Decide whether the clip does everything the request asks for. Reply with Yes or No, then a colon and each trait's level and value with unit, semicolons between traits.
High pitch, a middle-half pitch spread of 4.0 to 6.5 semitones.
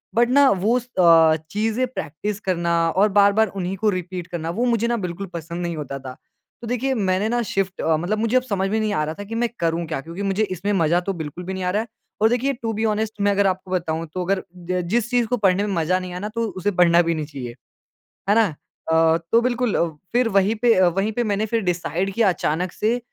Yes: high, 195 Hz; average, 4.3 semitones